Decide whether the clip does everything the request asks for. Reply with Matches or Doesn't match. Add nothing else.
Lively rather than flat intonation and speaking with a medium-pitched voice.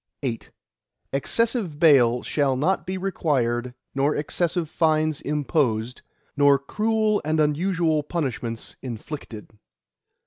Doesn't match